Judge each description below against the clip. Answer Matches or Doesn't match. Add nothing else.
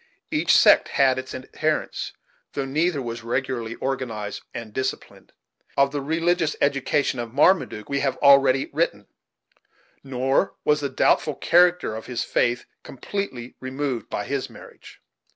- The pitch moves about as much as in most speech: Matches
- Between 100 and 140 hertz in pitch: Matches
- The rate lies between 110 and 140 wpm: Matches